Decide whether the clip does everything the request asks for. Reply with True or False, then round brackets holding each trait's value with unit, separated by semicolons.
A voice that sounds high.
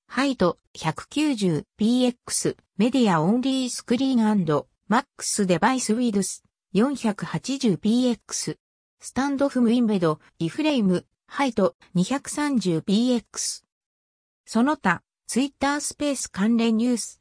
True (235 Hz)